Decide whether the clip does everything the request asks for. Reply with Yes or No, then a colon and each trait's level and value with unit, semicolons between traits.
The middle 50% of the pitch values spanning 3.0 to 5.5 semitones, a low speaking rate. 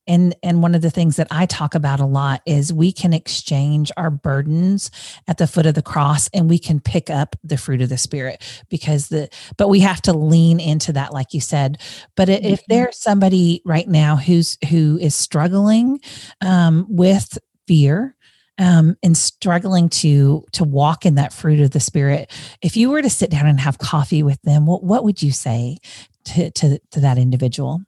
No: average, 3.5 semitones; average, 200 wpm